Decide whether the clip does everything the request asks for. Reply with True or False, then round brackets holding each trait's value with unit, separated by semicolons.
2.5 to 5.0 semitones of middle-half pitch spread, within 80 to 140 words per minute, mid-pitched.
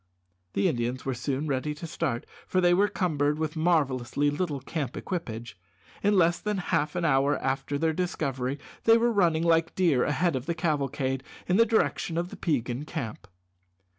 False (4.7 semitones; 175 wpm; 150 Hz)